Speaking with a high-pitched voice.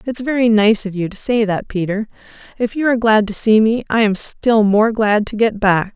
Yes: high, 215 Hz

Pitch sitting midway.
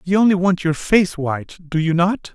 Yes: medium, 175 Hz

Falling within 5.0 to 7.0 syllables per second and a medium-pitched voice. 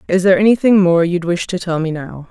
Yes: 6.1 syllables/s; medium, 180 Hz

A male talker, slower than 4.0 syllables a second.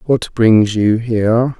Yes: male; 3.5 syllables/s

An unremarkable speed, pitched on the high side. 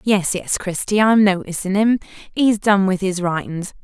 Yes: average, 170 wpm; high, 195 Hz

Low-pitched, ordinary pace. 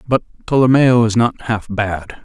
Yes: low, 115 Hz; average, 160 wpm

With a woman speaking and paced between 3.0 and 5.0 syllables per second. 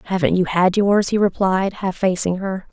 Yes: female; 4.7 syllables/s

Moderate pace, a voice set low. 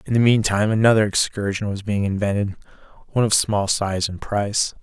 Yes: average, 185 wpm; low, 105 Hz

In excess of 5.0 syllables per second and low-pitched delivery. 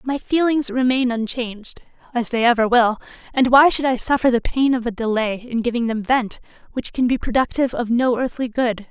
No: 5.4 syllables/s; high, 245 Hz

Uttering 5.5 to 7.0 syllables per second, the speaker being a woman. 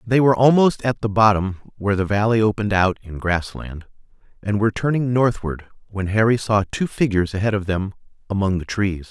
No: 5.8 syllables/s; male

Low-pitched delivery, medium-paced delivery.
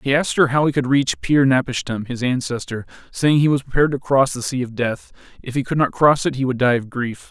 No: low, 130 Hz; fast, 280 wpm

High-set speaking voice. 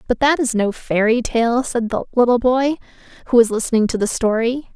Yes: high, 235 Hz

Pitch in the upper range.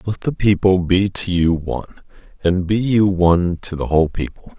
No: very low, 90 Hz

